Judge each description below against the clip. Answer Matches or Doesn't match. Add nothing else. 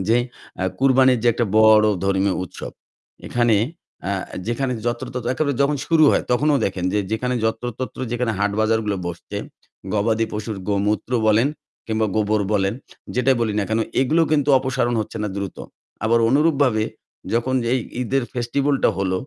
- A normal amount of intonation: Matches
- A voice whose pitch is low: Matches